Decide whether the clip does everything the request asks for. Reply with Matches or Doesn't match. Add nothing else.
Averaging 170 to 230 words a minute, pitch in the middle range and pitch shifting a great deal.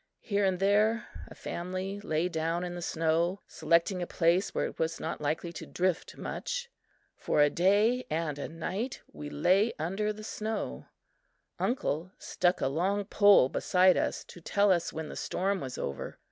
Doesn't match